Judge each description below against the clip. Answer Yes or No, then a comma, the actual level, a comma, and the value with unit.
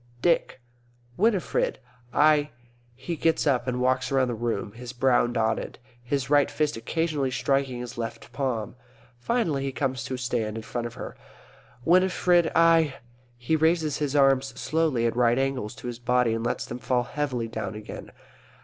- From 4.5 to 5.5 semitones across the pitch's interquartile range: No, average, 3.8 semitones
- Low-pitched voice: Yes, low, 130 Hz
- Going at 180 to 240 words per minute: No, average, 165 wpm